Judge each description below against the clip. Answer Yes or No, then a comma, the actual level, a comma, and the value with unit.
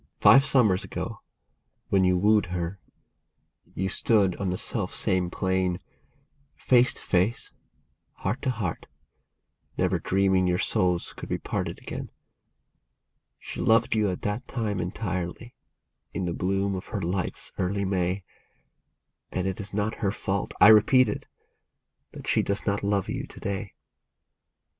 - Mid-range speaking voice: No, very low, 95 Hz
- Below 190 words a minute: Yes, average, 145 wpm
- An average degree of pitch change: No, narrow, 2.3 semitones